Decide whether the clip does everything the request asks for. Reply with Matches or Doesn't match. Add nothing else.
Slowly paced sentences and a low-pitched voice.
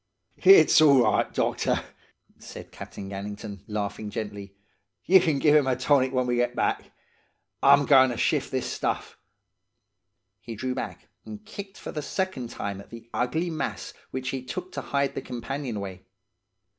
Doesn't match